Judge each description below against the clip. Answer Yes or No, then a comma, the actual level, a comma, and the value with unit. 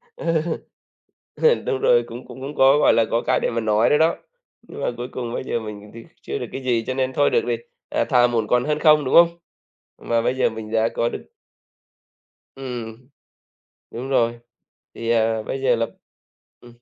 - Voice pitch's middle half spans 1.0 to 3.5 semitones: Yes, average, 2.8 semitones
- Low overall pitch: Yes, low, 120 Hz